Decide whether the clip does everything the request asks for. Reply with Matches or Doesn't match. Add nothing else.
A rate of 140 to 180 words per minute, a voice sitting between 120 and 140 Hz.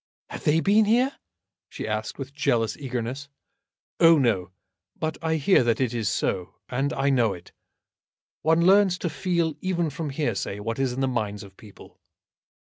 Matches